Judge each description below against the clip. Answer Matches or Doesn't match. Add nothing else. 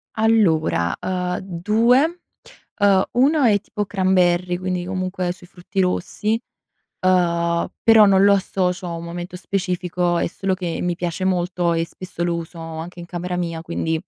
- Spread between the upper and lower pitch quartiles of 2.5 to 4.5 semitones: Doesn't match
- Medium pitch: Matches